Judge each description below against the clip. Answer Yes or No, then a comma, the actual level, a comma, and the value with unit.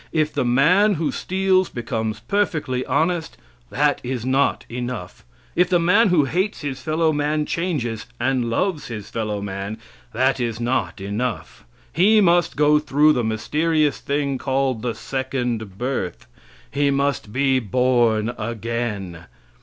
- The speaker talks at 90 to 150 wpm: Yes, average, 140 wpm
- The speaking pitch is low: Yes, low, 130 Hz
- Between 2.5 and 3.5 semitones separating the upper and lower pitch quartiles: No, average, 5.0 semitones